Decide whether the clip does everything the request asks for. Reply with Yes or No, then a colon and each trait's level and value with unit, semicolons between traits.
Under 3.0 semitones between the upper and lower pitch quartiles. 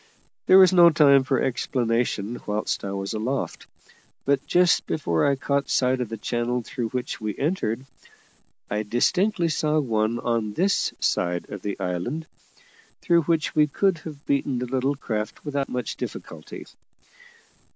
No: wide, 5.5 semitones